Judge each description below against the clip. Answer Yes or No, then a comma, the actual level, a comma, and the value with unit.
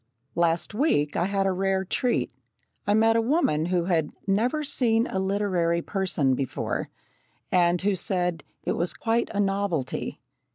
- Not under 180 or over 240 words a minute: No, average, 155 wpm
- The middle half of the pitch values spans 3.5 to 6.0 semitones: Yes, average, 3.8 semitones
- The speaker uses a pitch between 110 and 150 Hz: No, high, 190 Hz